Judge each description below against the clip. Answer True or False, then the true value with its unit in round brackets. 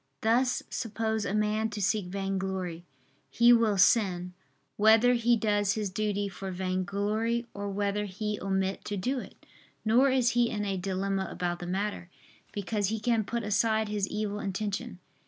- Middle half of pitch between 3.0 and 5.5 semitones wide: False (2.4 semitones)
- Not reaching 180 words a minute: True (160 wpm)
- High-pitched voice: True (205 Hz)